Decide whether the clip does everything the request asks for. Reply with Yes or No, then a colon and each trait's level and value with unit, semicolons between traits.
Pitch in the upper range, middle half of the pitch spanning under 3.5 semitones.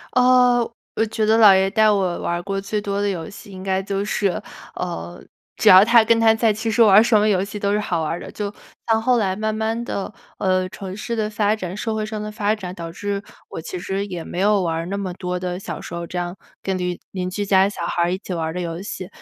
Yes: high, 200 Hz; average, 2.8 semitones